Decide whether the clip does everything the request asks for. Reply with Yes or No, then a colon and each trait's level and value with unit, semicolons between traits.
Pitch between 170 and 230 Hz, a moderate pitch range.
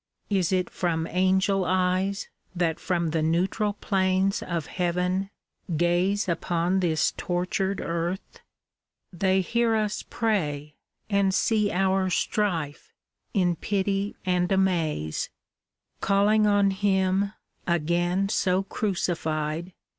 No: medium, 185 Hz; narrow, 2.3 semitones